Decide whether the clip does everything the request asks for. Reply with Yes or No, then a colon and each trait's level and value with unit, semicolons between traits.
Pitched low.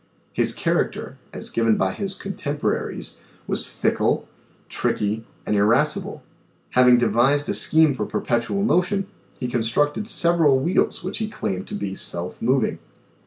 Yes: low, 130 Hz